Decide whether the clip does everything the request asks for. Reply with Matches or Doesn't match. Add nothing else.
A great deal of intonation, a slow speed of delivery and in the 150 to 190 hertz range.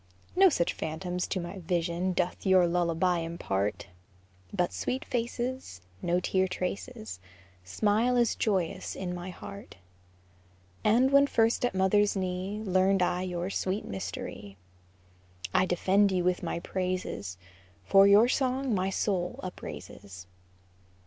Doesn't match